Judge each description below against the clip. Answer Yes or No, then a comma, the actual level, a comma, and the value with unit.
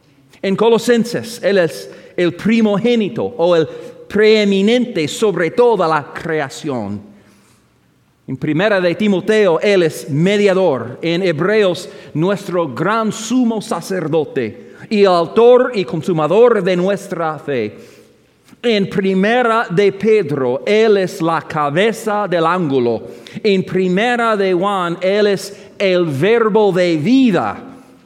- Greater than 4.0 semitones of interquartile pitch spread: Yes, average, 4.7 semitones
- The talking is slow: Yes, slow, 115 wpm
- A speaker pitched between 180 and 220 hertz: Yes, high, 190 Hz